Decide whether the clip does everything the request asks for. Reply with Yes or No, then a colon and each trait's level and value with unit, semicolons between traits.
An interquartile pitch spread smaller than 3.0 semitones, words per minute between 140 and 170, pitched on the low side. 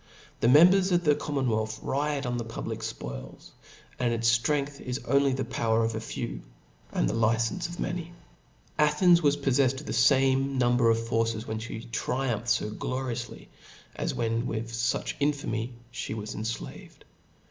No: average, 3.6 semitones; average, 165 wpm; low, 120 Hz